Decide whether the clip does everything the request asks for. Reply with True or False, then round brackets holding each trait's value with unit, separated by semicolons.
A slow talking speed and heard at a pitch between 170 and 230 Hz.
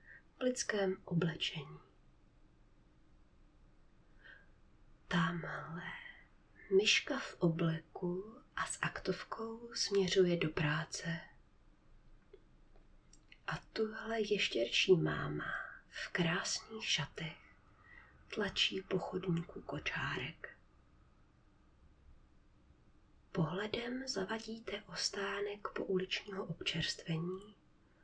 True (60 wpm; 190 Hz)